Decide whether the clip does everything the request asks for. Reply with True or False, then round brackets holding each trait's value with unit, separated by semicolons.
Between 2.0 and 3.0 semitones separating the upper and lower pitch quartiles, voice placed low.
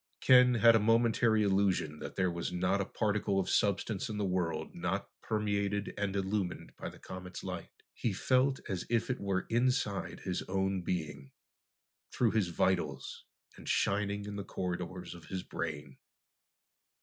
True (2.7 semitones; 100 Hz)